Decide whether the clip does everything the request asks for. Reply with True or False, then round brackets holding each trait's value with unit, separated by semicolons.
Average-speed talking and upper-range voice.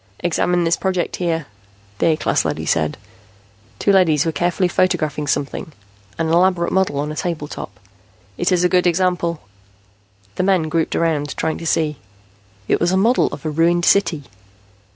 False (170 wpm; 170 Hz)